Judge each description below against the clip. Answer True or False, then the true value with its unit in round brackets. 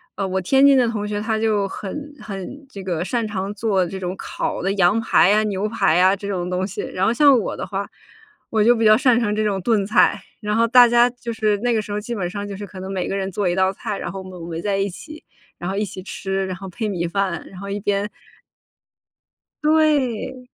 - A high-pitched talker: True (205 Hz)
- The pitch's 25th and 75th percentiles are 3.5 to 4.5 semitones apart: False (3.1 semitones)